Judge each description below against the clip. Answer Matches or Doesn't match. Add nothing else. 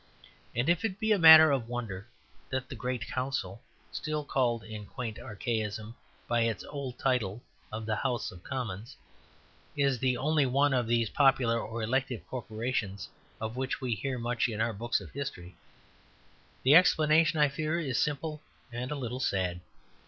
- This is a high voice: Doesn't match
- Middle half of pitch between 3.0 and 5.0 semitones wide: Matches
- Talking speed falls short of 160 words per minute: Doesn't match